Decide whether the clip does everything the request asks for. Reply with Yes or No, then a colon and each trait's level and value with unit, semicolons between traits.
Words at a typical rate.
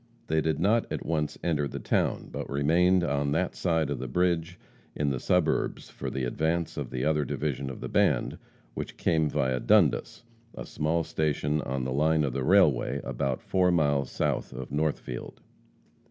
Yes: average, 180 wpm